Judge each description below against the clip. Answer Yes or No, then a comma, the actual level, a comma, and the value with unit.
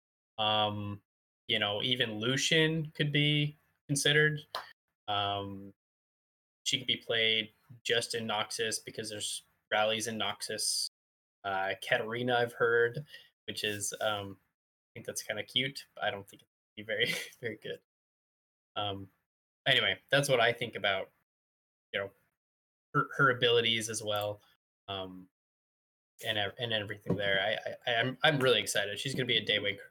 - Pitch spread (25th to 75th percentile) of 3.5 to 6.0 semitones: Yes, average, 3.9 semitones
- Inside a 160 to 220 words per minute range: No, average, 150 wpm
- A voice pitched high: No, low, 105 Hz